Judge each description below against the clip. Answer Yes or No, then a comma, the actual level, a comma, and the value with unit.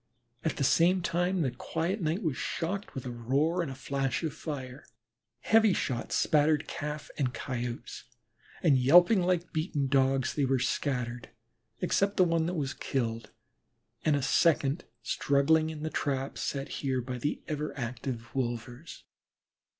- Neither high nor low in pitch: Yes, medium, 145 Hz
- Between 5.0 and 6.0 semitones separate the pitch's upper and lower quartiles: No, average, 4.2 semitones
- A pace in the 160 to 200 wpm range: No, average, 150 wpm